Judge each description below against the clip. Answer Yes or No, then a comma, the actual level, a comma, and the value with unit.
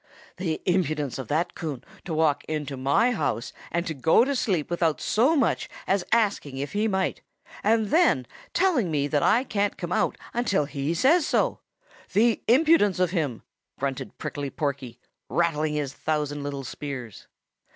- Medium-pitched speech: Yes, medium, 160 Hz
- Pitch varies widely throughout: Yes, wide, 6.4 semitones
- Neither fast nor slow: Yes, average, 160 wpm